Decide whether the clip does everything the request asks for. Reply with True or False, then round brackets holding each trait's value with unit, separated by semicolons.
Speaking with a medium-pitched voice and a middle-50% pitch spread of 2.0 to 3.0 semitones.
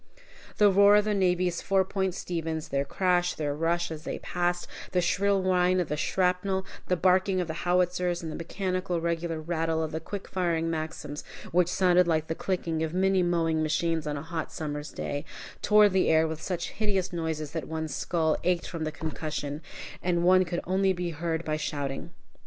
True (170 Hz; 2.5 semitones)